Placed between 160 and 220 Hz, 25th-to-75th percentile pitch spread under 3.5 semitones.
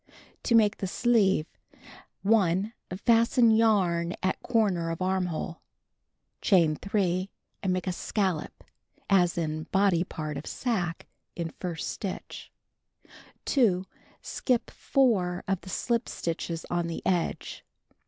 No: medium, 185 Hz; average, 4.2 semitones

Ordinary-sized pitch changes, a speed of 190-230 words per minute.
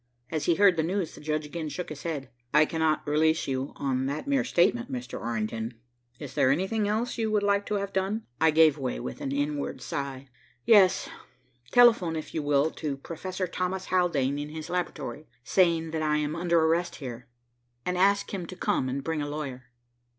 Yes: average, 4.6 semitones; average, 195 wpm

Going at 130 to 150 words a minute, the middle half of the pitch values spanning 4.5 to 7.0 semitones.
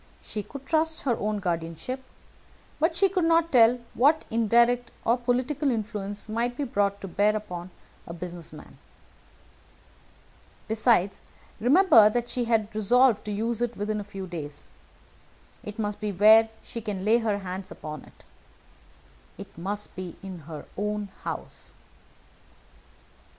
No: average, 145 wpm; average, 3.6 semitones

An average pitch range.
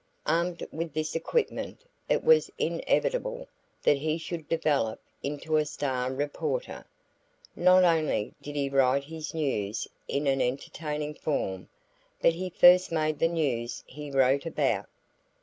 Yes: average, 3.4 semitones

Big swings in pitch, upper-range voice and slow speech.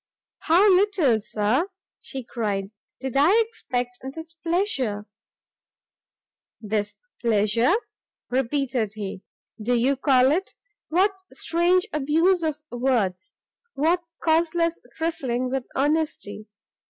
Yes: wide, 6.1 semitones; very high, 270 Hz; slow, 100 wpm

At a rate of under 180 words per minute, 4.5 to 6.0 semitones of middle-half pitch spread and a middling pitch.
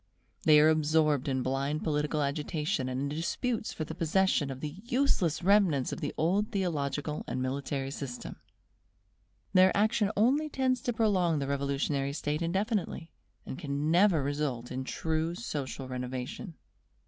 Yes: average, 150 wpm; average, 5.3 semitones; medium, 155 Hz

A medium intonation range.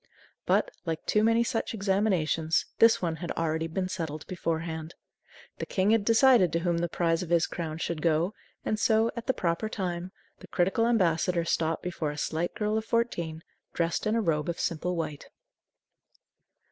Yes: average, 4.6 semitones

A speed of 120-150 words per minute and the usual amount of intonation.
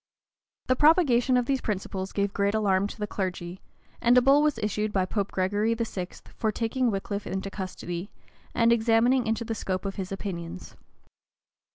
No: average, 170 wpm; average, 3.5 semitones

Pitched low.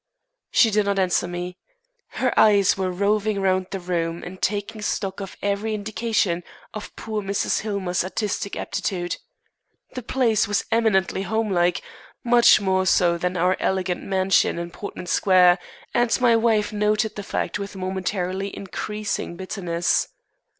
No: high, 195 Hz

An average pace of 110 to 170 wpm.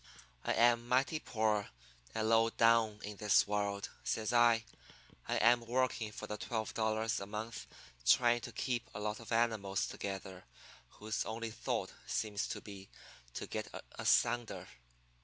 Yes: average, 145 wpm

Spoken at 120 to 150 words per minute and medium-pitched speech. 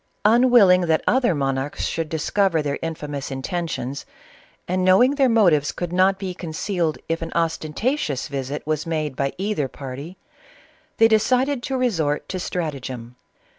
Yes: average, 145 wpm; medium, 165 Hz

